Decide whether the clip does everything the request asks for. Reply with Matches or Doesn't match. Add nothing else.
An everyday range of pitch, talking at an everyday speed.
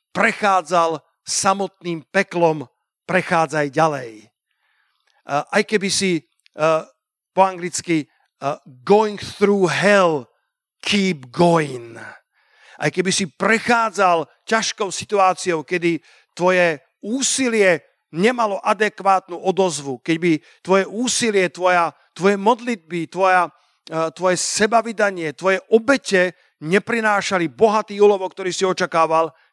Doesn't match